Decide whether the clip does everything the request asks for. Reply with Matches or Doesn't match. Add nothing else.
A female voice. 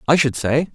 Doesn't match